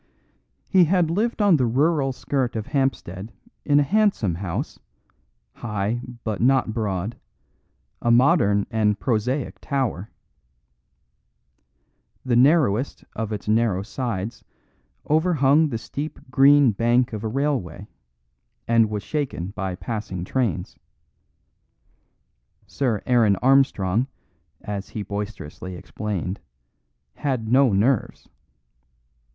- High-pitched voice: No, low, 115 Hz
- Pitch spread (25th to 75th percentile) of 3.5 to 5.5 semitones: Yes, average, 5.1 semitones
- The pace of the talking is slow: Yes, slow, 105 wpm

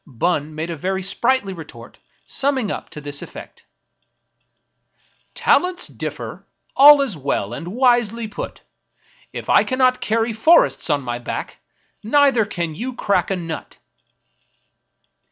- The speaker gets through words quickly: No, average, 140 wpm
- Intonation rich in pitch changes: Yes, wide, 8.3 semitones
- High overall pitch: Yes, high, 205 Hz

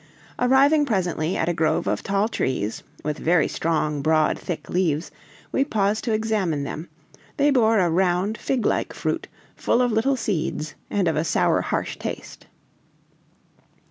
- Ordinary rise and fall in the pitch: No, wide, 5.9 semitones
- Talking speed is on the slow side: No, average, 155 wpm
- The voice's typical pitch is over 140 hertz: Yes, medium, 185 Hz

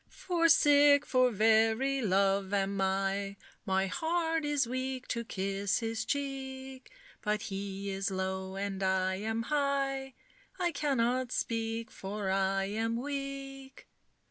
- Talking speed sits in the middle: No, slow, 125 wpm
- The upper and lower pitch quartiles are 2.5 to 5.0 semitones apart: No, wide, 5.6 semitones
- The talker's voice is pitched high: Yes, high, 225 Hz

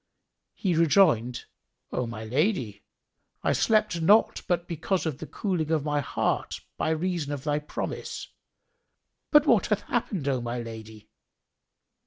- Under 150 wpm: Yes, average, 140 wpm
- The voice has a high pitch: No, medium, 155 Hz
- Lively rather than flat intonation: Yes, wide, 6.8 semitones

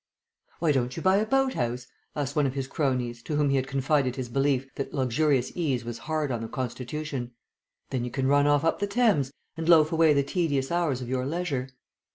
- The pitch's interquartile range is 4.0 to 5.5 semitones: No, average, 3.6 semitones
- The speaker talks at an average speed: No, fast, 215 wpm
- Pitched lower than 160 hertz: Yes, medium, 140 Hz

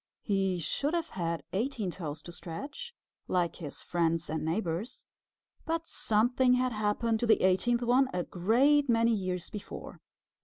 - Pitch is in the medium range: No, high, 210 Hz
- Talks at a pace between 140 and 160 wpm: Yes, average, 150 wpm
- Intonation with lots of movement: Yes, wide, 6.1 semitones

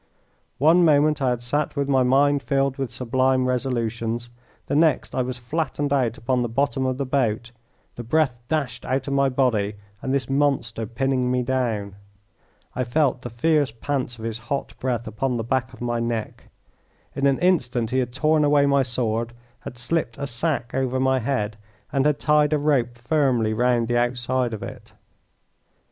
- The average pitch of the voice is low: Yes, low, 130 Hz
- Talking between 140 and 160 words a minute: No, average, 185 wpm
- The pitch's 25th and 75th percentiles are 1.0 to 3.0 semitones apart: Yes, average, 2.7 semitones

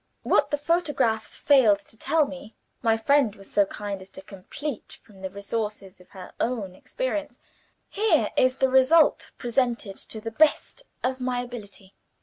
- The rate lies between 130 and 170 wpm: Yes, average, 160 wpm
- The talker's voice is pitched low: No, high, 230 Hz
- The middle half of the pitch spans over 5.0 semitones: Yes, wide, 5.6 semitones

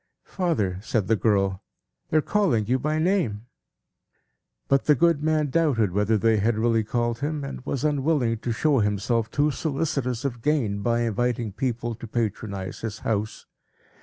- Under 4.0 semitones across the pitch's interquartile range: No, average, 5.2 semitones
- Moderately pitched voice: No, low, 120 Hz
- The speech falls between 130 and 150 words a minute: No, average, 165 wpm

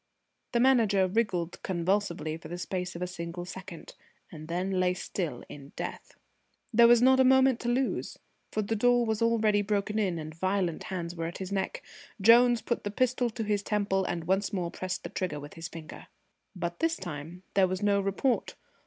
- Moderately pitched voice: No, high, 195 Hz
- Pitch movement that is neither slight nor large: Yes, average, 4.3 semitones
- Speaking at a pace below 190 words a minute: No, average, 195 wpm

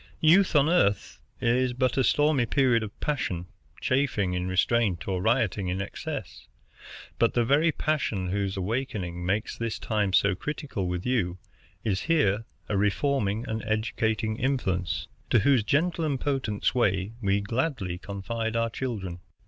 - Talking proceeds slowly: No, average, 145 wpm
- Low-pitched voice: Yes, low, 110 Hz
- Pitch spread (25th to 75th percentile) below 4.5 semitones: No, average, 5.3 semitones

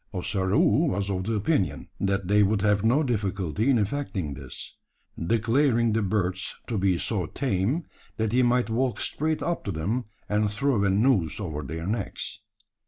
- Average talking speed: Yes, average, 170 wpm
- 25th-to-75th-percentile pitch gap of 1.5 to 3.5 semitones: No, average, 4.0 semitones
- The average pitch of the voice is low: Yes, low, 105 Hz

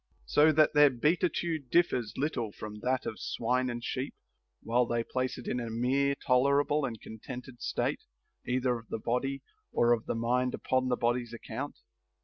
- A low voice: Yes, low, 125 Hz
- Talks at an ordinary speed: Yes, average, 170 wpm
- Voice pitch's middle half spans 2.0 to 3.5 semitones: Yes, average, 2.8 semitones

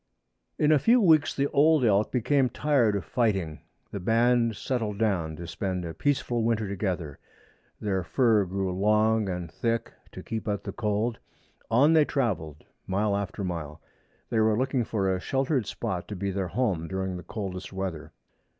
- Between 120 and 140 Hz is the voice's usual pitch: No, low, 105 Hz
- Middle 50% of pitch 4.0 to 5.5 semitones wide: Yes, average, 4.3 semitones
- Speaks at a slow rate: No, average, 170 wpm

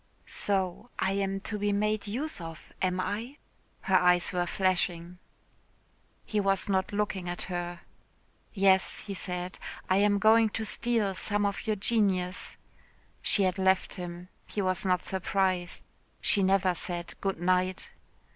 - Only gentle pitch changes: Yes, narrow, 2.1 semitones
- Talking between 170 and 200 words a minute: No, average, 145 wpm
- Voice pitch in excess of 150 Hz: Yes, high, 190 Hz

